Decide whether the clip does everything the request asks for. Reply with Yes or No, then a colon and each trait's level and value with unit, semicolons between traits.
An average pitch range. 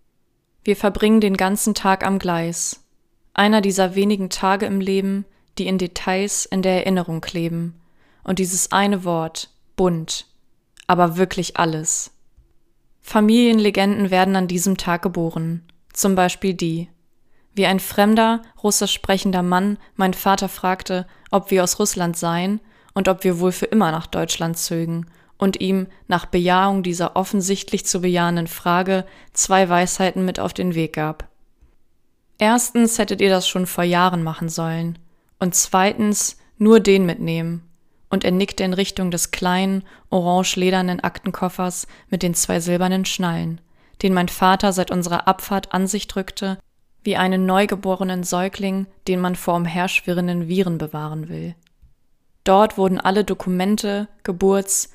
No: narrow, 1.9 semitones